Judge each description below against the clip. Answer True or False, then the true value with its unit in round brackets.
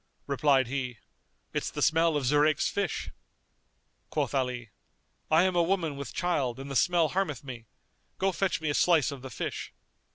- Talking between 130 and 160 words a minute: False (170 wpm)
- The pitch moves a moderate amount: True (4.3 semitones)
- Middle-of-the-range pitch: True (145 Hz)